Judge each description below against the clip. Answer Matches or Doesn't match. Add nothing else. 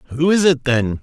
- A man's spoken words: Matches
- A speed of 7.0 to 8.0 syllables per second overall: Doesn't match